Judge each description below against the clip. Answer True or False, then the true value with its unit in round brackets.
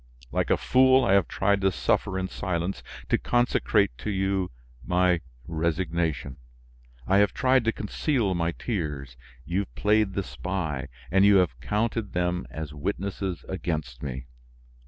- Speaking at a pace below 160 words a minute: True (150 wpm)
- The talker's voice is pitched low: True (95 Hz)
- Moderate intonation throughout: True (4.0 semitones)